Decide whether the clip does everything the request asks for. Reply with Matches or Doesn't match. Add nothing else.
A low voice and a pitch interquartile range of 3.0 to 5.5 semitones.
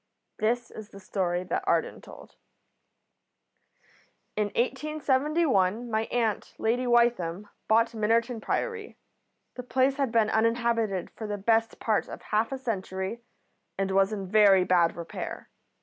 Doesn't match